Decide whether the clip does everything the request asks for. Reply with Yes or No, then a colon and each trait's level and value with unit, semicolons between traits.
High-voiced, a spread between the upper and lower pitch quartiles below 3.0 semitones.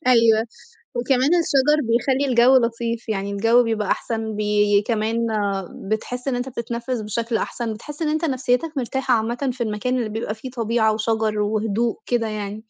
Yes: high, 230 Hz; narrow, 2.5 semitones